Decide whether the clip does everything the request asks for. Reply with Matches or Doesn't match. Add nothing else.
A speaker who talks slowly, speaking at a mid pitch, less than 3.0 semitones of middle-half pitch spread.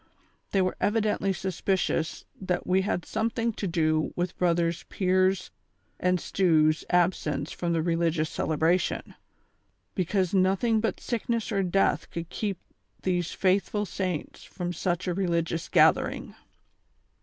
Matches